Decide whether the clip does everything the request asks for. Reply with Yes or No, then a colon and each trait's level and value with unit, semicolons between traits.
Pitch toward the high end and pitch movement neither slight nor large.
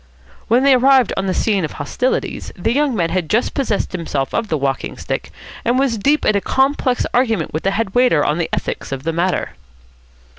No: high, 210 Hz; wide, 7.2 semitones